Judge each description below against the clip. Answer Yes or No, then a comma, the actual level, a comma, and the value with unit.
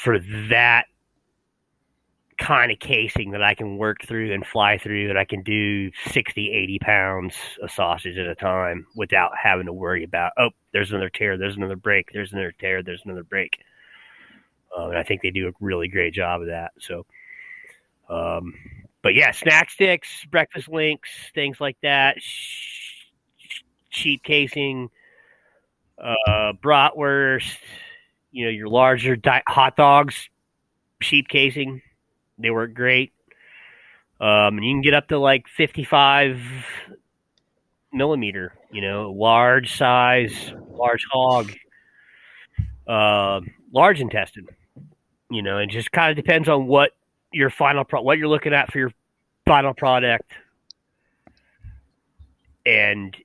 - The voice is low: Yes, low, 120 Hz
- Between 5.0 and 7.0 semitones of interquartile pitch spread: Yes, wide, 5.5 semitones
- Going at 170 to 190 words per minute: No, slow, 135 wpm